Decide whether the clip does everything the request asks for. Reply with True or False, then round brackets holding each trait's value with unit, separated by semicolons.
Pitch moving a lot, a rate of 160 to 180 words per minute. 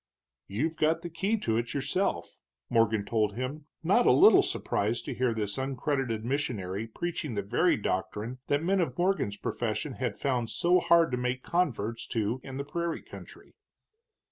True (6.5 semitones; 170 wpm)